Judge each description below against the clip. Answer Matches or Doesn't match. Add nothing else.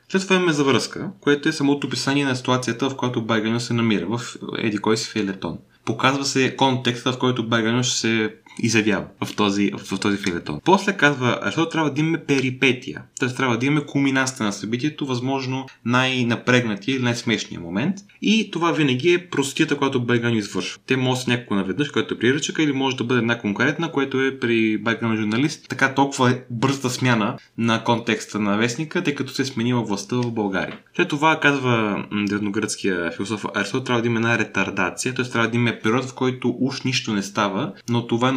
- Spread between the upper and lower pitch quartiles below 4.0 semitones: Matches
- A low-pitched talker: Matches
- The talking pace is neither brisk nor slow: Doesn't match